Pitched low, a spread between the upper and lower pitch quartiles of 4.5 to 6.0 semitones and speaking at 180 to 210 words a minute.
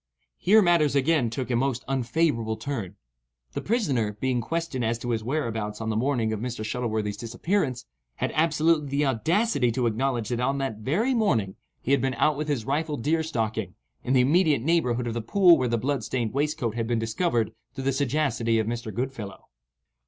Yes: low, 130 Hz; average, 4.8 semitones; average, 190 wpm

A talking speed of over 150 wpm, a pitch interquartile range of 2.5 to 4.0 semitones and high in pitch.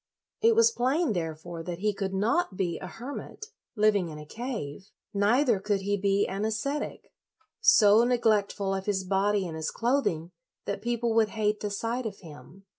Yes: average, 180 wpm; average, 3.5 semitones; high, 205 Hz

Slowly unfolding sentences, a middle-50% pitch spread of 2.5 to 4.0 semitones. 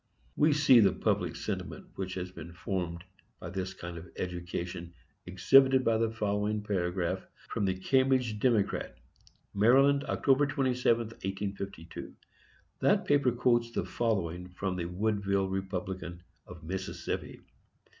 No: slow, 125 wpm; average, 4.7 semitones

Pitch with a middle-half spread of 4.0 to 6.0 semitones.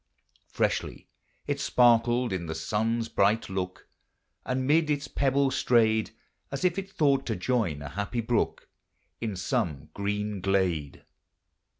Yes: average, 5.3 semitones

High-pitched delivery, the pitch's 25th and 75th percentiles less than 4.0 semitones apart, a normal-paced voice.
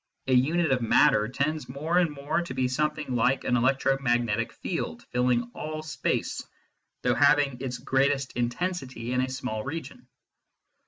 No: low, 130 Hz; average, 3.1 semitones; average, 150 wpm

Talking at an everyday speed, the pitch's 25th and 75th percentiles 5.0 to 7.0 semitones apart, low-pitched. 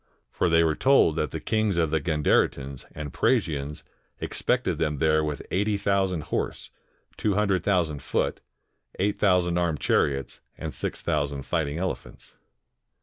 No: average, 145 wpm; average, 4.3 semitones; very low, 80 Hz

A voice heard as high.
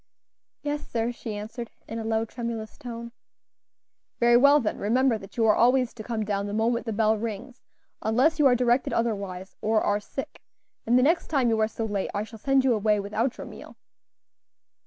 Yes: high, 230 Hz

